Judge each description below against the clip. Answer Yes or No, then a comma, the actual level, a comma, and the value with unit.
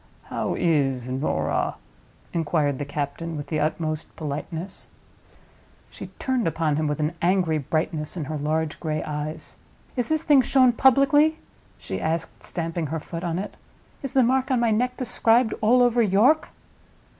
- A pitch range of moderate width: No, wide, 8.0 semitones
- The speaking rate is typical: Yes, average, 155 wpm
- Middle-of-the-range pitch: Yes, medium, 165 Hz